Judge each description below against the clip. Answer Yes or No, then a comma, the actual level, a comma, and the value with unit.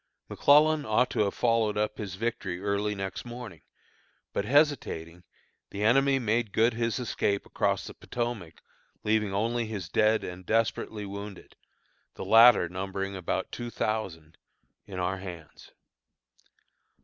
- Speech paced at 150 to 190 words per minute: No, slow, 135 wpm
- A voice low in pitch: Yes, low, 105 Hz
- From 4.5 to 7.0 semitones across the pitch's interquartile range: No, average, 3.4 semitones